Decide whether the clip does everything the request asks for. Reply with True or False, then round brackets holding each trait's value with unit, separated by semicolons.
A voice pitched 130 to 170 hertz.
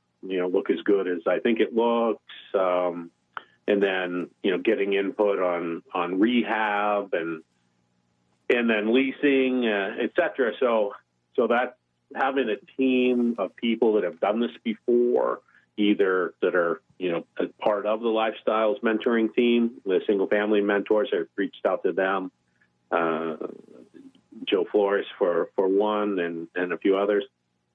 False (105 Hz)